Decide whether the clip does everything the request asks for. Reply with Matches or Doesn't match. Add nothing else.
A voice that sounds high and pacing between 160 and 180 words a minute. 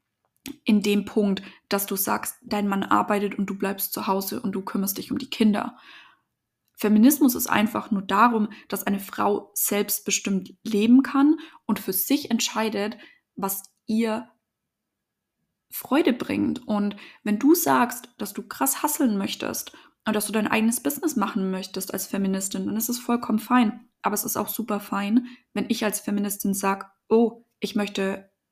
Matches